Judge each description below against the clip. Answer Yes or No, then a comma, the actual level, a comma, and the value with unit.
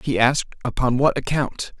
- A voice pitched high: No, low, 130 Hz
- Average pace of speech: Yes, average, 165 wpm